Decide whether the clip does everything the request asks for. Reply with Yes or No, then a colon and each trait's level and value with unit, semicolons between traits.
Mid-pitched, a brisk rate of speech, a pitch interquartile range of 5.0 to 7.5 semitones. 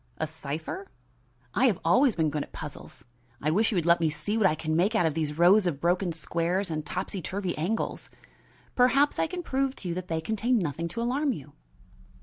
Yes: medium, 175 Hz; fast, 215 wpm; wide, 5.6 semitones